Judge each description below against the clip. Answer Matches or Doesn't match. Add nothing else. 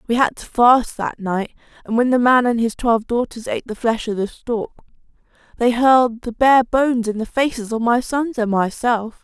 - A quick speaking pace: Matches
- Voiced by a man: Doesn't match